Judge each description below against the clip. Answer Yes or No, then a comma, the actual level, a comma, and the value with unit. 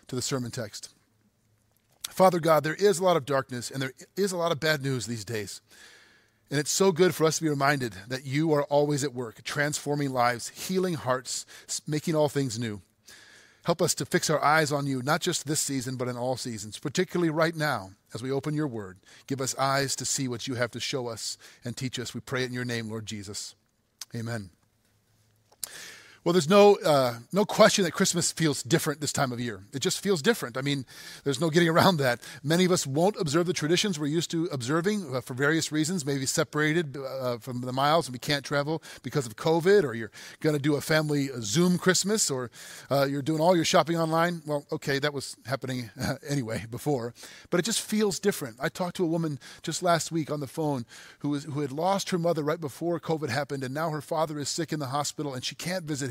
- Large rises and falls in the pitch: No, average, 4.7 semitones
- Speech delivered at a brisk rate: Yes, fast, 225 wpm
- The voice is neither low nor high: Yes, medium, 145 Hz